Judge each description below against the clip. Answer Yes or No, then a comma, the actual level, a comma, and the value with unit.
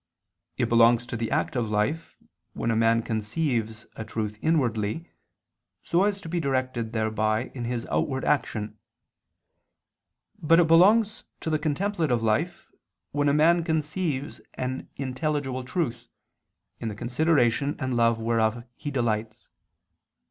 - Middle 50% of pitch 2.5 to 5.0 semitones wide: No, wide, 5.5 semitones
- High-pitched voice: No, low, 130 Hz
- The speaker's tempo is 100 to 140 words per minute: Yes, slow, 135 wpm